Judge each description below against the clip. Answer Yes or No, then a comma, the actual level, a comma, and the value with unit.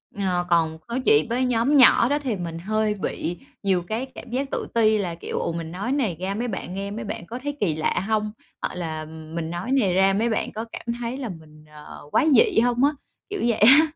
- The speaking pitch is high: Yes, high, 210 Hz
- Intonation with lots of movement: Yes, wide, 5.9 semitones